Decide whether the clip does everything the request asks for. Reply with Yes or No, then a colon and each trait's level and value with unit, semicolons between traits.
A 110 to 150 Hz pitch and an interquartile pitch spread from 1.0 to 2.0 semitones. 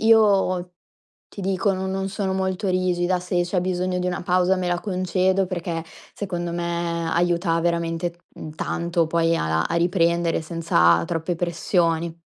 No: medium, 175 Hz; narrow, 1.7 semitones